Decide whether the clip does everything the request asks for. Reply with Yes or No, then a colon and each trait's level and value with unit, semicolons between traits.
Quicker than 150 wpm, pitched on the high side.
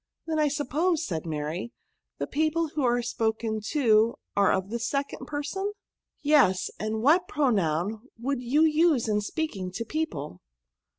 Yes: average, 160 wpm; high, 245 Hz